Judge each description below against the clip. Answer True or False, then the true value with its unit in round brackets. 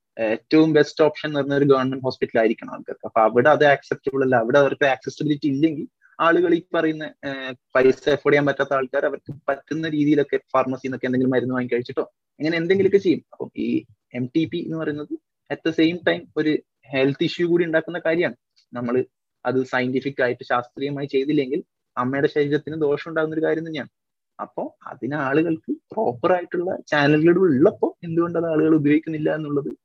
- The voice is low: False (145 Hz)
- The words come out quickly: True (155 wpm)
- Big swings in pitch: False (3.4 semitones)